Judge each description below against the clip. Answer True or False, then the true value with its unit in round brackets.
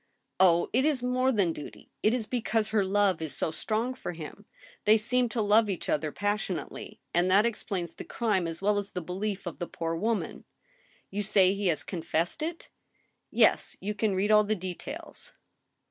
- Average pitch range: True (3.6 semitones)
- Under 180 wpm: False (195 wpm)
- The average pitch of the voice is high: True (205 Hz)